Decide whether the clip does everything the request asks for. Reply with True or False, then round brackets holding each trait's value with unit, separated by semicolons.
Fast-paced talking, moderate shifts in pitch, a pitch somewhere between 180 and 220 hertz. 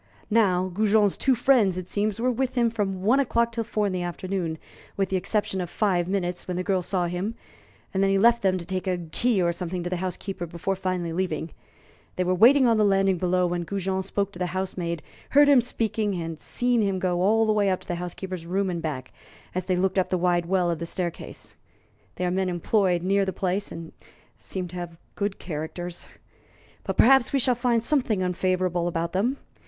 True (220 wpm; 3.0 semitones; 185 Hz)